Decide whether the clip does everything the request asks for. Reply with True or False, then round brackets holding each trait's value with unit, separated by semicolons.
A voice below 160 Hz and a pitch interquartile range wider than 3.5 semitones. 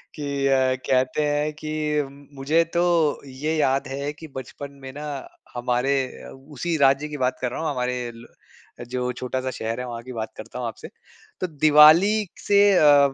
False (140 Hz; 3.1 semitones)